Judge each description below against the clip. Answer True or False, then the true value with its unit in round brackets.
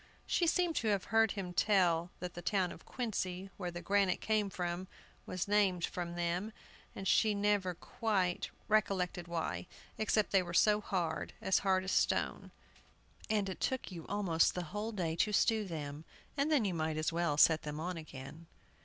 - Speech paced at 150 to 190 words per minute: True (180 wpm)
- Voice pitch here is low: False (185 Hz)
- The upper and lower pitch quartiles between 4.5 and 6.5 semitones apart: False (3.4 semitones)